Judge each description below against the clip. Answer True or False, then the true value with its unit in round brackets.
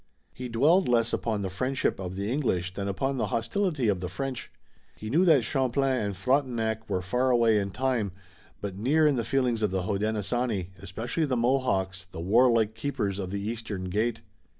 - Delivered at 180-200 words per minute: True (185 wpm)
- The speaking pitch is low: True (115 Hz)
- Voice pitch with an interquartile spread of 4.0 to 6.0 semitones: True (4.6 semitones)